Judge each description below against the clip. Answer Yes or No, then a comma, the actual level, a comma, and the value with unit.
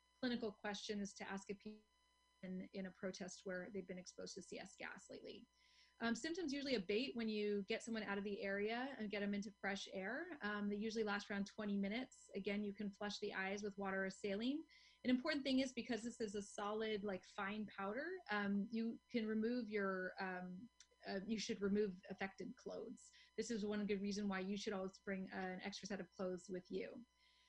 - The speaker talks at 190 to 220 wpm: Yes, fast, 205 wpm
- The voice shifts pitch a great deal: No, average, 2.7 semitones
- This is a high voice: Yes, high, 205 Hz